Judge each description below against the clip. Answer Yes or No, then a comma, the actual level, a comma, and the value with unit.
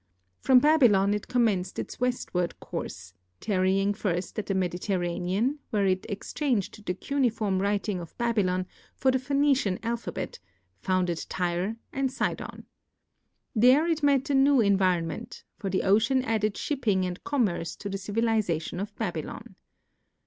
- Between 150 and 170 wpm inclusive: No, slow, 135 wpm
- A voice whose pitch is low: No, high, 205 Hz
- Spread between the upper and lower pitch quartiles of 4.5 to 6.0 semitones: Yes, average, 5.2 semitones